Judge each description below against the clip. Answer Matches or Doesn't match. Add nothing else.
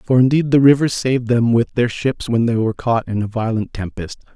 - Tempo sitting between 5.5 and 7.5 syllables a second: Matches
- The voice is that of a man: Matches